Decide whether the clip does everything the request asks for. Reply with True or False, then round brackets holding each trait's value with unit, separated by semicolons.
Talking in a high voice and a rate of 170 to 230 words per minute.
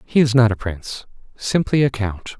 False (120 Hz; 200 wpm)